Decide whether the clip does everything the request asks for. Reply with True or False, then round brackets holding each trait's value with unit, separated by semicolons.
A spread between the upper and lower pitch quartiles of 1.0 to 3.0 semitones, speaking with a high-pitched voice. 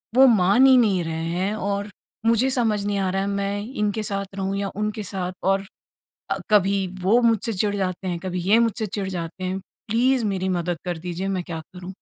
True (2.5 semitones; 195 Hz)